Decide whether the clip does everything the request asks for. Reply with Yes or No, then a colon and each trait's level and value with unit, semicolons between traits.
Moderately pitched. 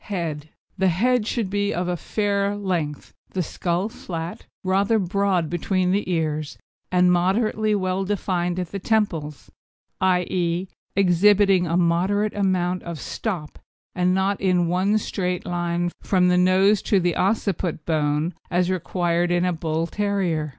Yes: medium, 180 Hz